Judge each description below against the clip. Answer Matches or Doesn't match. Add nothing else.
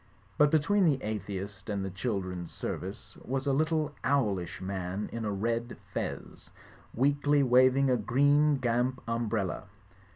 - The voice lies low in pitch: Matches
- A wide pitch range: Matches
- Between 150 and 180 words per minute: Doesn't match